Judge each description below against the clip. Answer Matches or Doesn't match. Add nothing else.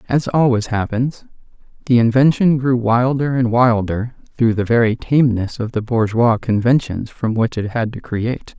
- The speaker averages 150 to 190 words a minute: Matches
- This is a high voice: Doesn't match